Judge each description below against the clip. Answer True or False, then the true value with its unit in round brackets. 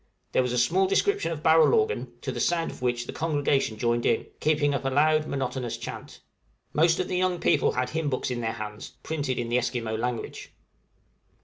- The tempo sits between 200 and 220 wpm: True (205 wpm)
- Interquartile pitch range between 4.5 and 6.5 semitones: True (5.1 semitones)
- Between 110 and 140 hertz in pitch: True (135 Hz)